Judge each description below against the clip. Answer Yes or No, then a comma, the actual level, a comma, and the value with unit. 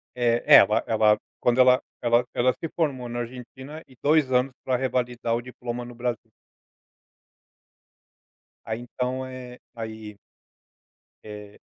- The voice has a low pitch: Yes, low, 125 Hz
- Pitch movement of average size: No, narrow, 1.7 semitones